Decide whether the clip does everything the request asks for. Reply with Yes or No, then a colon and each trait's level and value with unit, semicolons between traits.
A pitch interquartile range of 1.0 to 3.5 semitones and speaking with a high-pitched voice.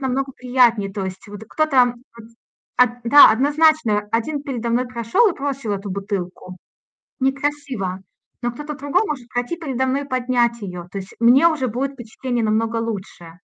No: average, 4.2 semitones; high, 245 Hz